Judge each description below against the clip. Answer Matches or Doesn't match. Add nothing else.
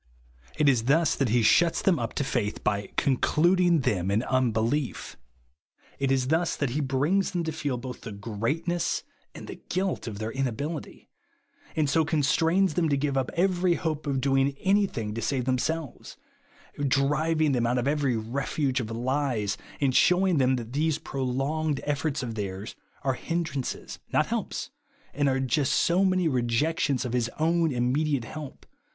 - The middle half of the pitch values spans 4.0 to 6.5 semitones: Matches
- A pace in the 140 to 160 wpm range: Doesn't match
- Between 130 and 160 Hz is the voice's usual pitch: Matches